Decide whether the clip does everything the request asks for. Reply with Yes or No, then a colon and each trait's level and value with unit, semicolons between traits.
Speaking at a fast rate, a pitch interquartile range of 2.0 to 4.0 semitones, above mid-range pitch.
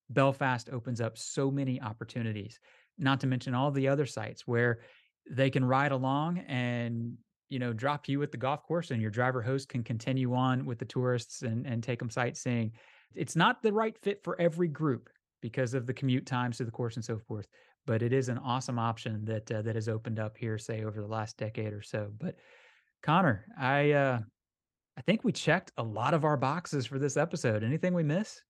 No: fast, 210 wpm; average, 3.6 semitones; low, 130 Hz